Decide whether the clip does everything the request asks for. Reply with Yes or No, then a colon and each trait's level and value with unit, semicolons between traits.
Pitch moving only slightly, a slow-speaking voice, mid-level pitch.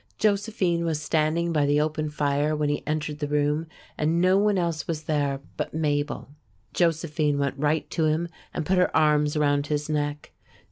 No: narrow, 2.1 semitones; average, 180 wpm; medium, 155 Hz